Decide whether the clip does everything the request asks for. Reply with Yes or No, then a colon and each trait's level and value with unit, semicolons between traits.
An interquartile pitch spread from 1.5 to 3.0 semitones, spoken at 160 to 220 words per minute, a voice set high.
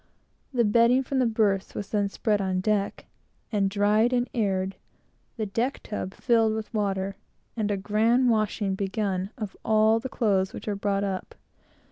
Yes: narrow, 2.4 semitones; average, 165 wpm; high, 210 Hz